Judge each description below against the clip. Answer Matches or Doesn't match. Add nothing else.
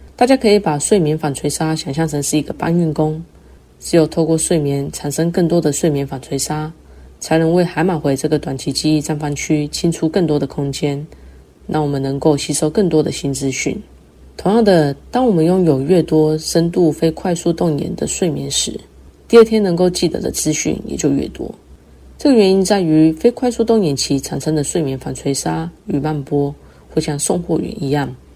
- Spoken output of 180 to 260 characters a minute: Doesn't match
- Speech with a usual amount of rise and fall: Matches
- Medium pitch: Matches